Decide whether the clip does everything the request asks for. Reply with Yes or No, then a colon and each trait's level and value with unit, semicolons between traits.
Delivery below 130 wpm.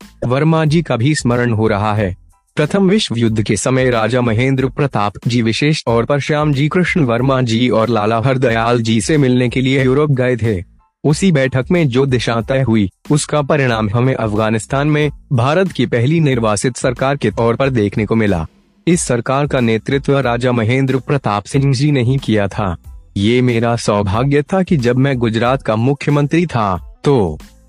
No: average, 180 wpm